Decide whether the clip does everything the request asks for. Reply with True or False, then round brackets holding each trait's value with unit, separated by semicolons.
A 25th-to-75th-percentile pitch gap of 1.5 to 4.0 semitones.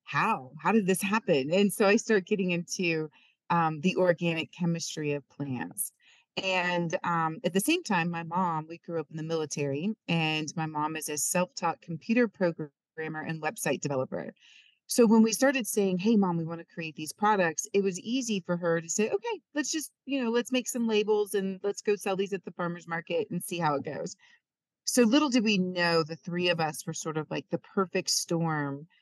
False (4.7 semitones)